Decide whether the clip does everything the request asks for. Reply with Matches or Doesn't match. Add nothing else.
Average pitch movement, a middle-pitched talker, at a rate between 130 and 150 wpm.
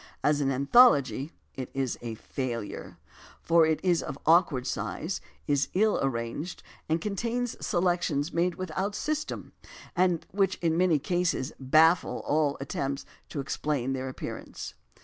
Matches